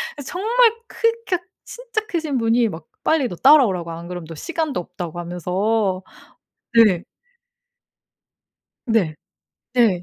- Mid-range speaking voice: No, high, 225 Hz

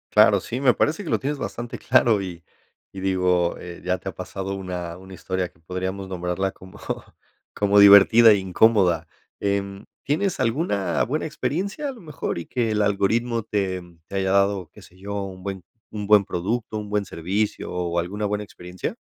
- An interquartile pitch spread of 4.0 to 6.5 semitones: No, average, 2.9 semitones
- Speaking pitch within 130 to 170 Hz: No, low, 100 Hz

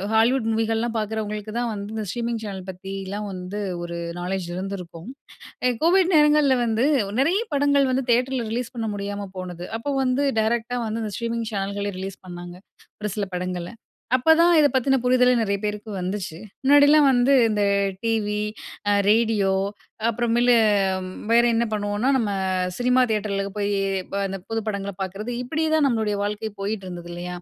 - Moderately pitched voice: No, high, 220 Hz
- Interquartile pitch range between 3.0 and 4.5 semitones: Yes, average, 3.8 semitones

